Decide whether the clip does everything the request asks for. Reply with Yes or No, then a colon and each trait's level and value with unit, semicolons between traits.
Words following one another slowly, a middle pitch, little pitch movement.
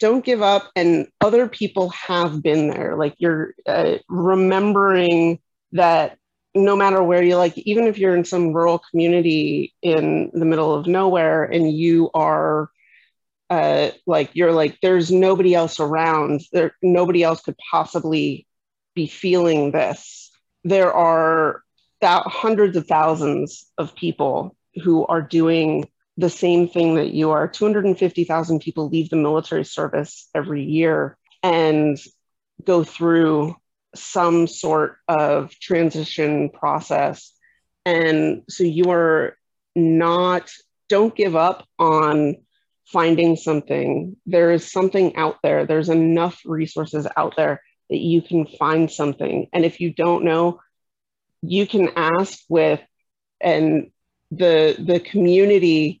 Yes: slow, 130 wpm; medium, 170 Hz; narrow, 2.3 semitones